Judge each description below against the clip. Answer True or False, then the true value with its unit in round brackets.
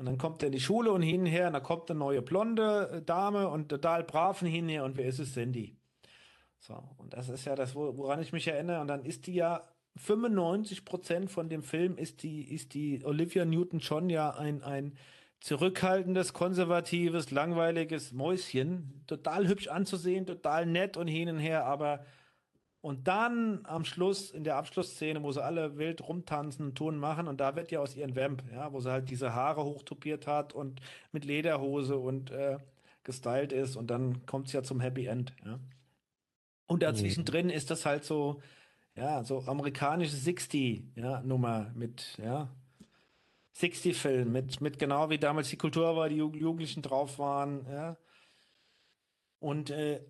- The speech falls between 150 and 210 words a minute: True (175 wpm)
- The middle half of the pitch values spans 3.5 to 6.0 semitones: True (3.8 semitones)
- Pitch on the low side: False (150 Hz)